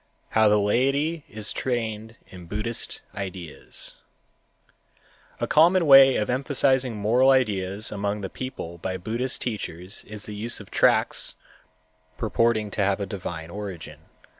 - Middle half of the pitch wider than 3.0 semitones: Yes, average, 4.2 semitones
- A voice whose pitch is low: Yes, low, 110 Hz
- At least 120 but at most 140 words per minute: Yes, slow, 135 wpm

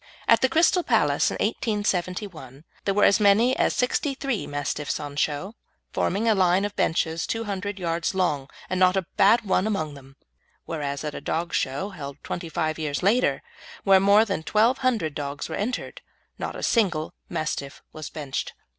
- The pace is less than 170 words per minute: No, average, 180 wpm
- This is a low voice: No, medium, 185 Hz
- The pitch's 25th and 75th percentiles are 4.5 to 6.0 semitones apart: Yes, average, 5.3 semitones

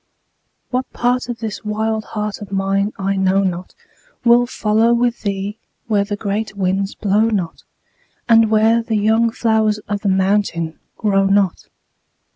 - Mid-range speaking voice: No, high, 210 Hz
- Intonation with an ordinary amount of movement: No, narrow, 2.2 semitones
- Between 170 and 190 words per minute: No, average, 150 wpm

